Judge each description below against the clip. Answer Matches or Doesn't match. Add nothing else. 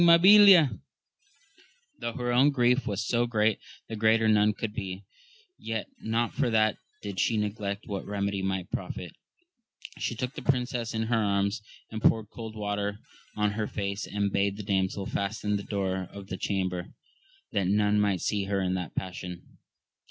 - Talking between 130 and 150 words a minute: Doesn't match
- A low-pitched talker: Matches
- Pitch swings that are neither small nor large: Doesn't match